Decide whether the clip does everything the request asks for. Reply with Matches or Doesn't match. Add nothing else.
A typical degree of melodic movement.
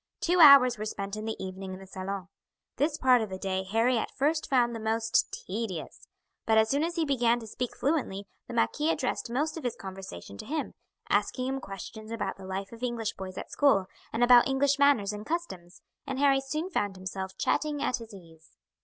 Doesn't match